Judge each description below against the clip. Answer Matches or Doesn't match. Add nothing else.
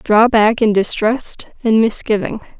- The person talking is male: Doesn't match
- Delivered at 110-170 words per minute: Matches